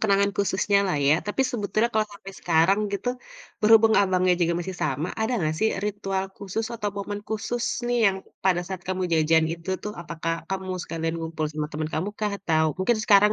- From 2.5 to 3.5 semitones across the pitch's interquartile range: No, average, 4.0 semitones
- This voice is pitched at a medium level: No, high, 195 Hz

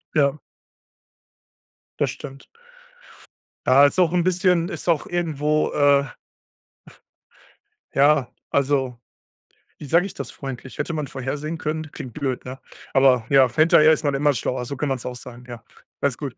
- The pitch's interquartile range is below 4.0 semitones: Yes, average, 2.8 semitones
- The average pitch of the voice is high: No, medium, 140 Hz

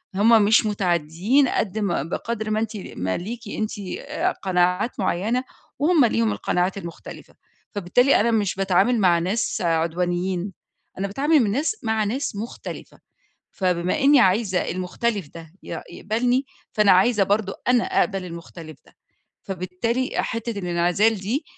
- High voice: Yes, high, 200 Hz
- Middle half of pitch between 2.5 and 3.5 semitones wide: No, average, 4.5 semitones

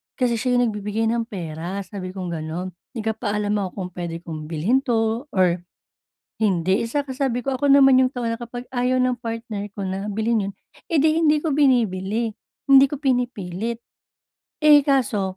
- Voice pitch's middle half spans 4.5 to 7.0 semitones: Yes, average, 4.9 semitones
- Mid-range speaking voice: No, high, 225 Hz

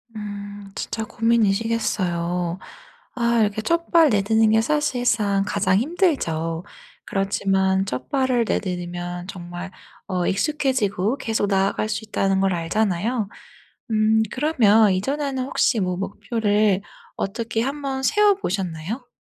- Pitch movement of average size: Yes, average, 3.8 semitones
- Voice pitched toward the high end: Yes, high, 210 Hz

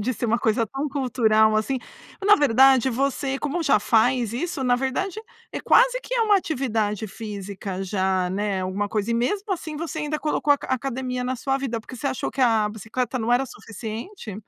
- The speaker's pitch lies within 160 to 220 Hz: No, very high, 250 Hz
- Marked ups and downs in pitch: No, average, 4.2 semitones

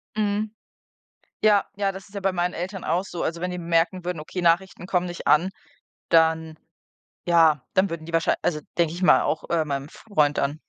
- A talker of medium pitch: Yes, medium, 175 Hz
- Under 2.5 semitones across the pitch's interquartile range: No, average, 2.8 semitones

